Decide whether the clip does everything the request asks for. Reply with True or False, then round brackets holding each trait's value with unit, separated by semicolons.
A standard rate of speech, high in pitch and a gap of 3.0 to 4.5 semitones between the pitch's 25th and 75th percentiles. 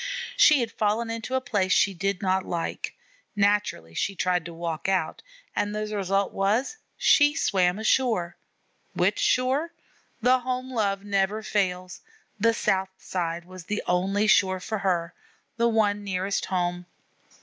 True (150 wpm; 200 Hz; 3.4 semitones)